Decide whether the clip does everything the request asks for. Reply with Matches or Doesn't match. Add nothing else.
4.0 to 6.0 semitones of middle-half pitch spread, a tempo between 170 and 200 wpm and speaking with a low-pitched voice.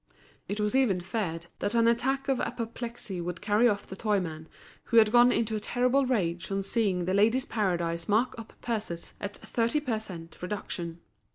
Doesn't match